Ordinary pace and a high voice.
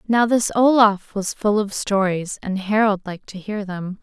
Yes: average, 195 wpm; high, 205 Hz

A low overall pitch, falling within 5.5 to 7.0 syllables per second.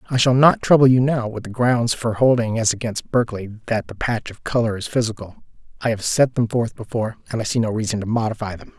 Yes: low, 115 Hz; 6.0 syllables/s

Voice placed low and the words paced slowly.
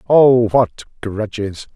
Yes: low, 115 Hz; slow, 105 wpm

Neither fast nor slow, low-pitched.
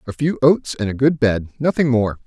No: fast, 210 wpm; low, 125 Hz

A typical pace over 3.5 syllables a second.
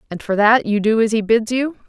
Yes: 5.7 syllables/s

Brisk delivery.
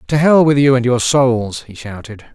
Yes: fast, 230 wpm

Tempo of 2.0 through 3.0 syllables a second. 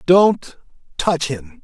Yes: 2.7 syllables/s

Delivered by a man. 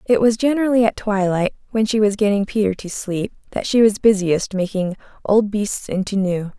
No: female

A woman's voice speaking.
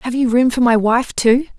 Yes: female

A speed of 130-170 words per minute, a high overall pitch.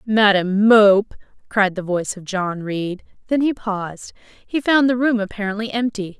Yes: average, 165 wpm; high, 210 Hz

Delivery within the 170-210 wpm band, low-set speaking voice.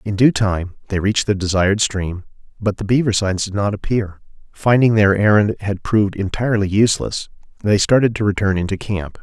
Yes: average, 180 wpm; low, 100 Hz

